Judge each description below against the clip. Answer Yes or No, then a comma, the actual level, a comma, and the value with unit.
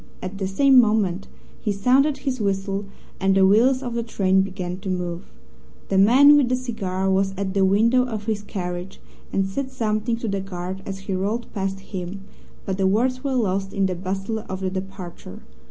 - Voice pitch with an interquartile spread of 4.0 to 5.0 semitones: No, average, 3.3 semitones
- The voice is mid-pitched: No, high, 195 Hz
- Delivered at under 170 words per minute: No, average, 195 wpm